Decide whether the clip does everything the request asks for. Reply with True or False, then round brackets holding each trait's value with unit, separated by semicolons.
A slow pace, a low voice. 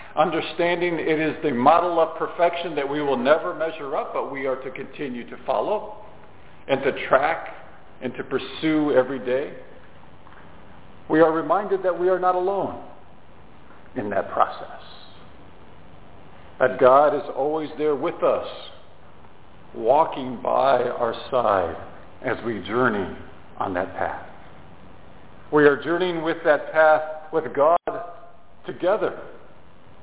False (130 wpm; 155 Hz)